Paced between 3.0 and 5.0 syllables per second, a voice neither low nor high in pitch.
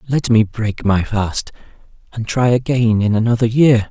No: 4.5 syllables/s; low, 115 Hz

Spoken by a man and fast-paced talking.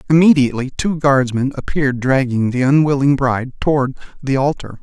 No: male; slow, 135 wpm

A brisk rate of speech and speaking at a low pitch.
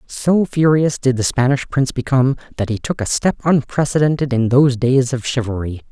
No: average, 185 wpm; low, 130 Hz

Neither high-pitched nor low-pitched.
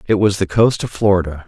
No: low, 100 Hz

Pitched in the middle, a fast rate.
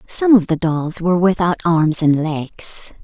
No: medium, 170 Hz; average, 180 wpm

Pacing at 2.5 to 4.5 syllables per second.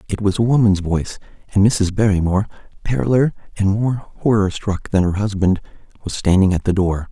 No: 5.4 syllables/s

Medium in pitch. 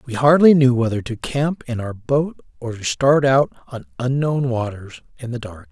No: low, 125 Hz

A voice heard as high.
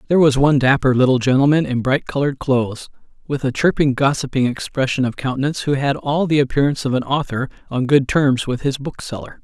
No: low, 135 Hz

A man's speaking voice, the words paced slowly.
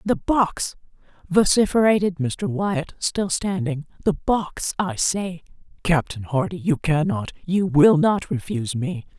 No: female; slow, 125 wpm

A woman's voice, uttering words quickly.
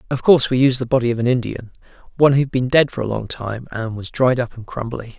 No: male; fast, 280 wpm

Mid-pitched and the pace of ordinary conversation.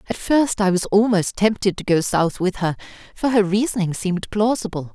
No: high, 200 Hz; average, 195 wpm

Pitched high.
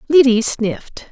Yes: very high, 250 Hz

